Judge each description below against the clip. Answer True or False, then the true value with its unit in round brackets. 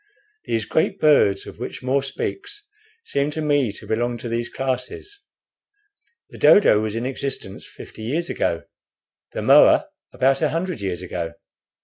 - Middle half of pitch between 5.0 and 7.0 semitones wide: True (5.5 semitones)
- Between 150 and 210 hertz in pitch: False (130 Hz)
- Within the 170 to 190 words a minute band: False (150 wpm)